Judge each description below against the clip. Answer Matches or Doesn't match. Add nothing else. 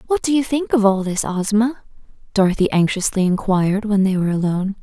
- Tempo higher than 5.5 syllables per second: Matches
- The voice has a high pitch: Matches